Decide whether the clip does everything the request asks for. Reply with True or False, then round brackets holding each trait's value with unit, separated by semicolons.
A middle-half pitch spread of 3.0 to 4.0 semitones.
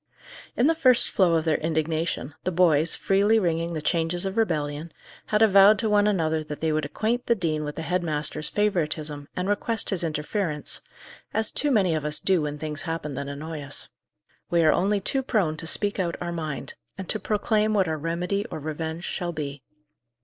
False (4.6 semitones)